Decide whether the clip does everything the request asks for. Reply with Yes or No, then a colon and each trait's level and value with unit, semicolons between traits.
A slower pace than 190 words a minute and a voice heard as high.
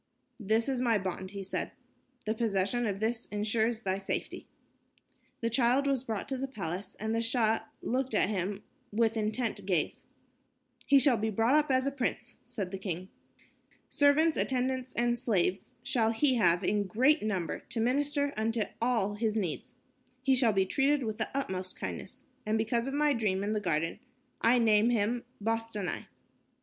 Yes: average, 170 wpm; high, 225 Hz